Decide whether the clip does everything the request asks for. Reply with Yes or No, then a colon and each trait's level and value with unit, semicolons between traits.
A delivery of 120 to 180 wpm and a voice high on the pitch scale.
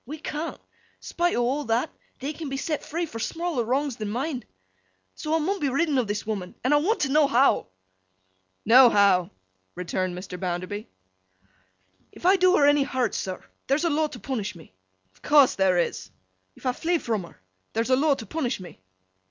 No: average, 195 wpm; very high, 260 Hz